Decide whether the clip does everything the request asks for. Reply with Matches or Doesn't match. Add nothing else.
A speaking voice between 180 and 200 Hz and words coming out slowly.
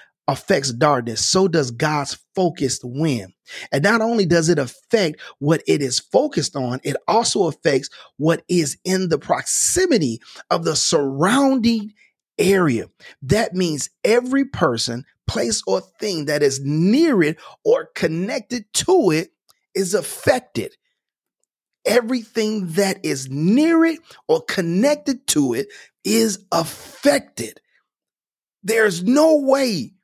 Matches